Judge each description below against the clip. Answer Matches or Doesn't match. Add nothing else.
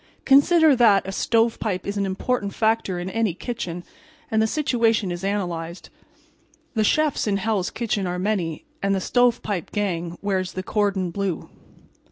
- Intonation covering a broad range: Doesn't match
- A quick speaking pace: Doesn't match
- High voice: Matches